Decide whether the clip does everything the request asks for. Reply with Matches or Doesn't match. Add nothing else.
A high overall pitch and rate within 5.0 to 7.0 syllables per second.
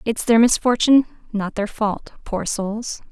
Doesn't match